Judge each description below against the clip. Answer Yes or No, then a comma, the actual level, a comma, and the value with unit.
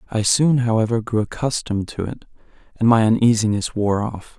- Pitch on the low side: Yes, low, 110 Hz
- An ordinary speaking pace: Yes, average, 165 wpm